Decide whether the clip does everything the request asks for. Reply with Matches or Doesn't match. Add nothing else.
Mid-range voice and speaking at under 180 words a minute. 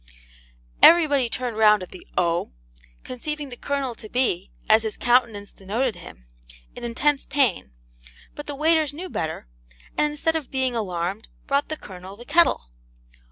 Doesn't match